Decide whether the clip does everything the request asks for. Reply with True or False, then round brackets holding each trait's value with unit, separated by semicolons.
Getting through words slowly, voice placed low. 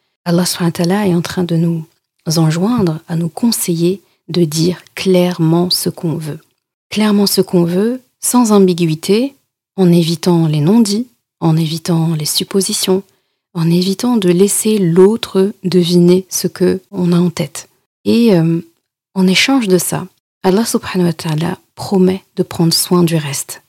False (135 wpm; 180 Hz)